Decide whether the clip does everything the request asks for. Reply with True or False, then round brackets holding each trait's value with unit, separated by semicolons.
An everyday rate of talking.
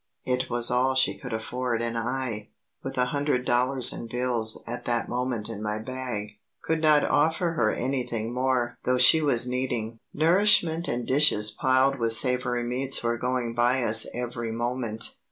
True (170 wpm)